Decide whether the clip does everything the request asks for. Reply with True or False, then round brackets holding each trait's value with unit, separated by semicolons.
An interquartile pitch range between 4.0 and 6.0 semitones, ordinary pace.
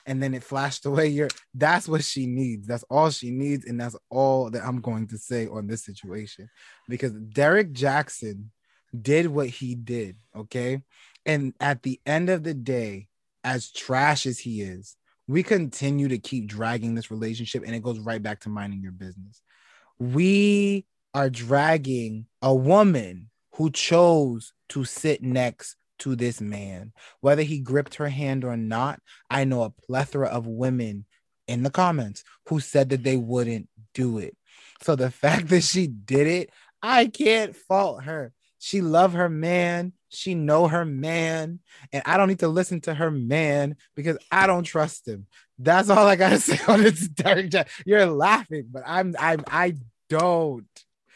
True (5.5 semitones; 170 wpm)